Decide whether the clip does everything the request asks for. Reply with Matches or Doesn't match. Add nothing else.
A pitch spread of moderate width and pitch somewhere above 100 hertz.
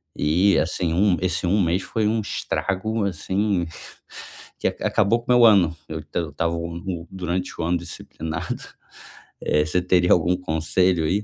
Doesn't match